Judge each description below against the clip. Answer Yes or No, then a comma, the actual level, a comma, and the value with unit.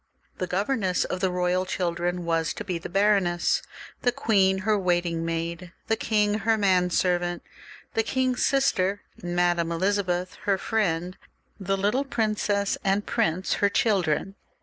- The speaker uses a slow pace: No, average, 145 wpm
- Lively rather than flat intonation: No, average, 2.8 semitones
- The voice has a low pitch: No, medium, 185 Hz